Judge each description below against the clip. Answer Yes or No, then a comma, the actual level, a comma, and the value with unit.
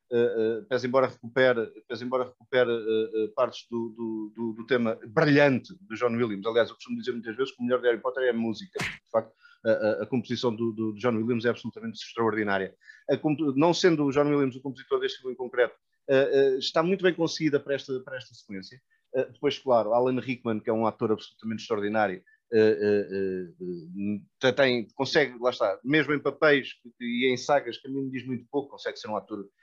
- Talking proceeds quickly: Yes, fast, 215 wpm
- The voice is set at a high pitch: No, low, 125 Hz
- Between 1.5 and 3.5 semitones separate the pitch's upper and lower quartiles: No, average, 4.2 semitones